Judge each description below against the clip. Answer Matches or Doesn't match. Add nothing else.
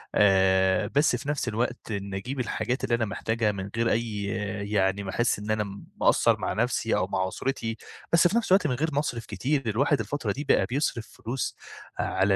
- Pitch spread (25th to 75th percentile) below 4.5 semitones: Doesn't match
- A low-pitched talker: Matches